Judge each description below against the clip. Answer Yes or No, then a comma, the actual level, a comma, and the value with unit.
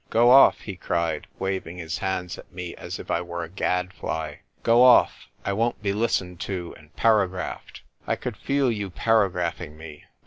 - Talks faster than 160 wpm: Yes, average, 180 wpm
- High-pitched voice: No, very low, 90 Hz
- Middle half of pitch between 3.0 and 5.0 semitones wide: Yes, average, 4.1 semitones